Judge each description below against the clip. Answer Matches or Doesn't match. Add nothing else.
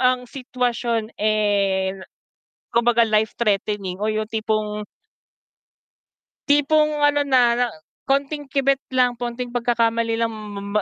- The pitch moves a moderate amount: Matches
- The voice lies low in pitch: Doesn't match